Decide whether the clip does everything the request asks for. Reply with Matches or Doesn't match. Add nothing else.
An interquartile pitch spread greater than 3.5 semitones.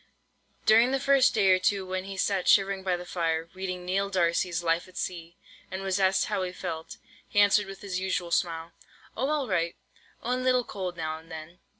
Doesn't match